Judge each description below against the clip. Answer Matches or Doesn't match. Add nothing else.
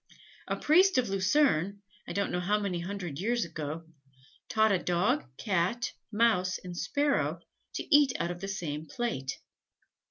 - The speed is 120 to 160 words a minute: Matches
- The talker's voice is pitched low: Doesn't match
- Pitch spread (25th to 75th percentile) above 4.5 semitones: Matches